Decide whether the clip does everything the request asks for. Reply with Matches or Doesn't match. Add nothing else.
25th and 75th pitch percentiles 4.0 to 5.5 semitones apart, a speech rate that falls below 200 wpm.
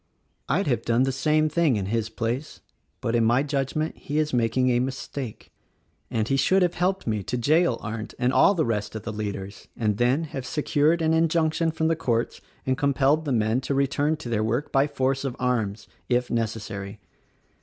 Doesn't match